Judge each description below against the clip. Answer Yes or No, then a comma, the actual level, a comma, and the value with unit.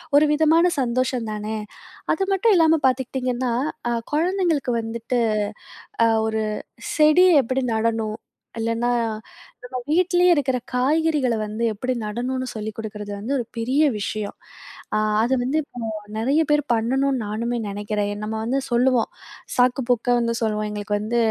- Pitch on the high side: Yes, high, 245 Hz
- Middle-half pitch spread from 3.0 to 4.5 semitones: Yes, average, 4.2 semitones